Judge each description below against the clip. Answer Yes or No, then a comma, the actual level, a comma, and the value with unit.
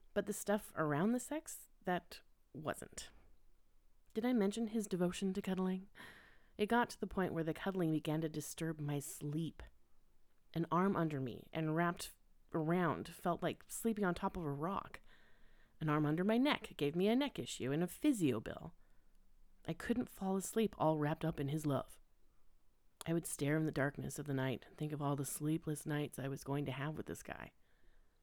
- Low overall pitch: No, medium, 165 Hz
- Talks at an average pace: Yes, average, 195 wpm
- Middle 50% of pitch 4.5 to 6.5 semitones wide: Yes, average, 5.0 semitones